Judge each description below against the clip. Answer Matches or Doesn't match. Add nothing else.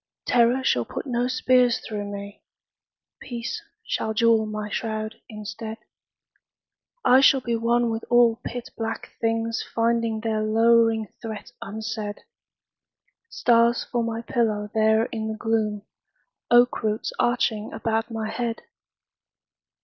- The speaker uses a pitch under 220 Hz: Doesn't match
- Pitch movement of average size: Doesn't match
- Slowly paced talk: Matches